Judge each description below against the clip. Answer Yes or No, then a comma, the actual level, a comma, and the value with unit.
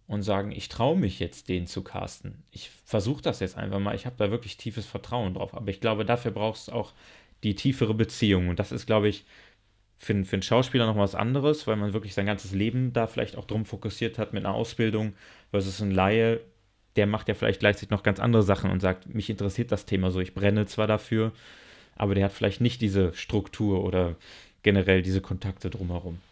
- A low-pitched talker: Yes, low, 105 Hz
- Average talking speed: No, fast, 220 wpm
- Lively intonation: No, narrow, 2.5 semitones